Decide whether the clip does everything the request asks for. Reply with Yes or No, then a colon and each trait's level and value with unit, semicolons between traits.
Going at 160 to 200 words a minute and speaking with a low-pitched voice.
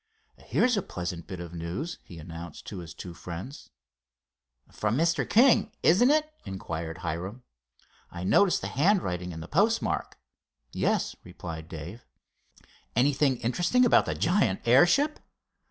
No: slow, 135 wpm; low, 100 Hz